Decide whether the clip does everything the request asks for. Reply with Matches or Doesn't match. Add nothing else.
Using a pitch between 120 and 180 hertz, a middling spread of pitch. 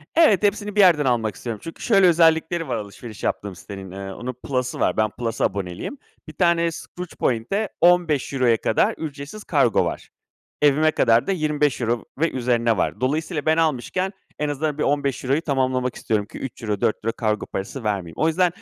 Doesn't match